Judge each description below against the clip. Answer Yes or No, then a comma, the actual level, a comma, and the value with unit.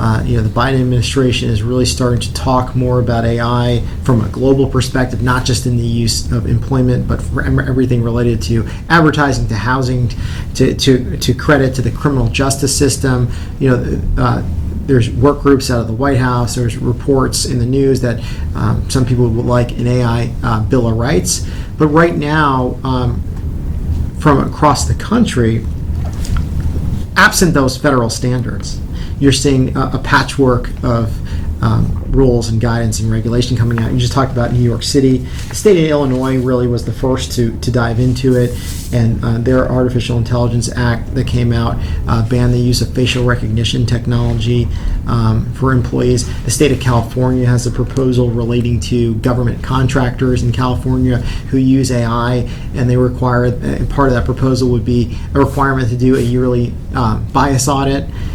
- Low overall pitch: Yes, low, 120 Hz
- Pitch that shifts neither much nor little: No, narrow, 2.0 semitones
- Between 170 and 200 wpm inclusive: Yes, average, 175 wpm